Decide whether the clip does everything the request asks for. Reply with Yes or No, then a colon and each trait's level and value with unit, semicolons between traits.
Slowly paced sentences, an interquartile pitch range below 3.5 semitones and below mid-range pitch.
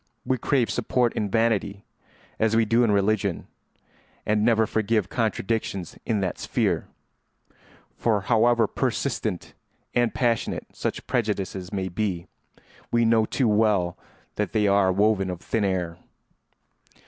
Yes: slow, 130 wpm; average, 2.8 semitones; low, 105 Hz